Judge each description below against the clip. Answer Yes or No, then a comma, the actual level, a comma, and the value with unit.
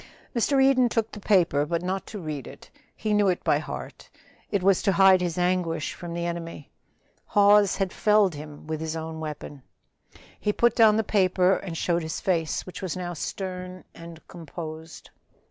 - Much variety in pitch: No, average, 3.6 semitones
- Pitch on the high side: No, medium, 180 Hz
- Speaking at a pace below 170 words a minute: No, average, 180 wpm